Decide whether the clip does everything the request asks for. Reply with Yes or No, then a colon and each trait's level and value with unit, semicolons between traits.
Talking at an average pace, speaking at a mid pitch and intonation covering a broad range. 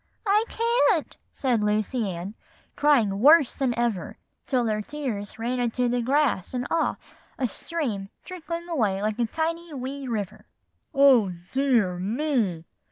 No: average, 145 wpm; high, 245 Hz; wide, 5.8 semitones